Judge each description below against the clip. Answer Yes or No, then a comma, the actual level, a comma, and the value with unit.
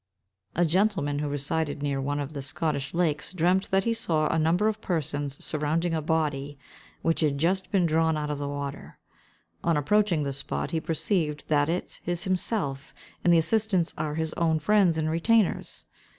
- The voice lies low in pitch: No, medium, 160 Hz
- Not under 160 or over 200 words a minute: Yes, average, 180 wpm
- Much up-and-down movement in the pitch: No, average, 3.4 semitones